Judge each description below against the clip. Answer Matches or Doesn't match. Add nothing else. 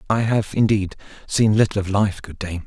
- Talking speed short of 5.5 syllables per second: Matches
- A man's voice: Matches